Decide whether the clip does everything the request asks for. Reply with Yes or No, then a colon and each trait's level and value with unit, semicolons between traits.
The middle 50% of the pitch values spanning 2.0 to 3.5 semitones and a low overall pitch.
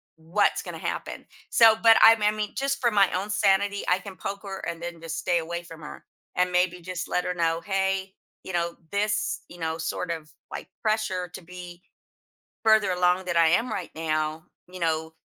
No: average, 3.2 semitones; medium, 180 Hz